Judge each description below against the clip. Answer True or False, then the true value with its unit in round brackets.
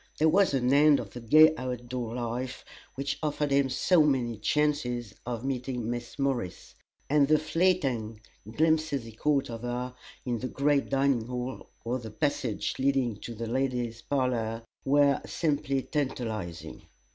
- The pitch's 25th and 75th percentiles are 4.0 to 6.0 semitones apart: False (3.2 semitones)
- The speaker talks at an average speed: True (155 wpm)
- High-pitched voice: False (130 Hz)